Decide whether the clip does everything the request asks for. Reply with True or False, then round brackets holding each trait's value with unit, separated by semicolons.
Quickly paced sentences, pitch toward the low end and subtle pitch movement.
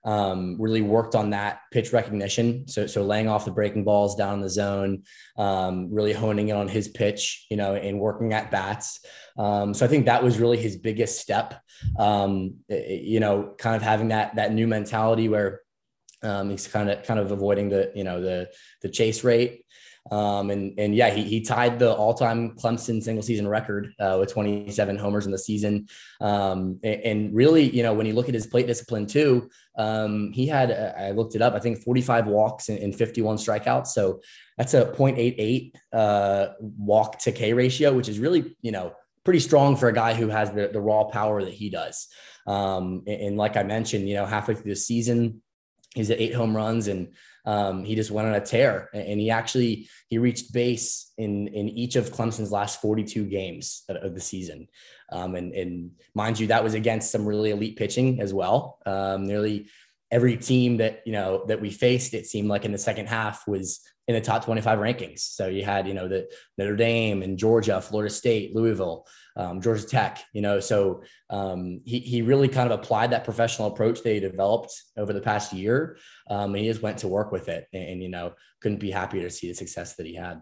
True (210 wpm; 105 Hz; 2.3 semitones)